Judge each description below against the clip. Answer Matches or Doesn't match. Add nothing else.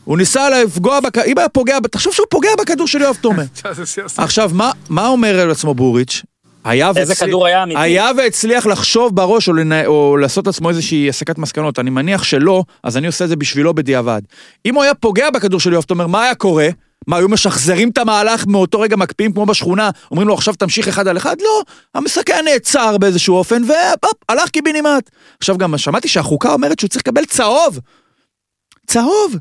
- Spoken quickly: Matches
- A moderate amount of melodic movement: Doesn't match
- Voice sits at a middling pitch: Doesn't match